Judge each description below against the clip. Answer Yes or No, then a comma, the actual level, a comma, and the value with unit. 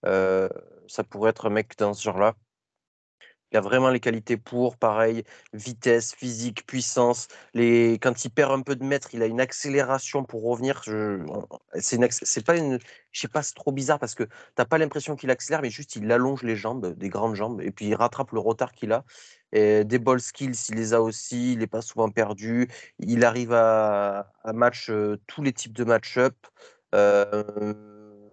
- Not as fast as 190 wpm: No, average, 200 wpm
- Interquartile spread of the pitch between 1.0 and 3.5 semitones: Yes, average, 2.8 semitones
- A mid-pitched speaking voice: No, low, 120 Hz